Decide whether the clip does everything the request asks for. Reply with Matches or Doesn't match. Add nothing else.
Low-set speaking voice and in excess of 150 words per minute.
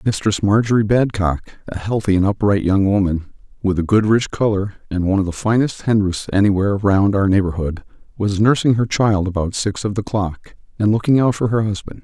Matches